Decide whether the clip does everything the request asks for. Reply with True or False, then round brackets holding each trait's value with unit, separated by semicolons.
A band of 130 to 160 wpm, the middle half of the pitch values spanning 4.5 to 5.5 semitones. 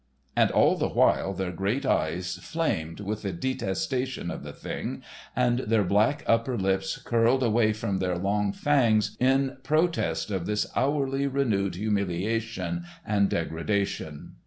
True (140 wpm; 5.2 semitones)